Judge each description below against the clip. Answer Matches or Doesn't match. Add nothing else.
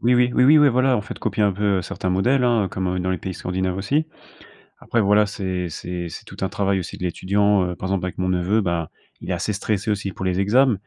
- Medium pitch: Doesn't match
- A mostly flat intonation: Doesn't match